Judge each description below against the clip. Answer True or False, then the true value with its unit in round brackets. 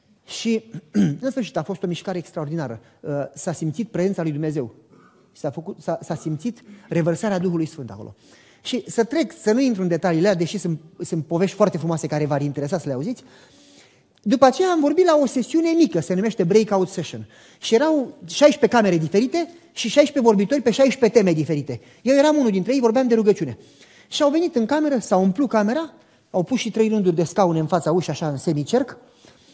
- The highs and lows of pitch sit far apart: True (6.7 semitones)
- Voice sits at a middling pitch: False (195 Hz)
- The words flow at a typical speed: False (195 wpm)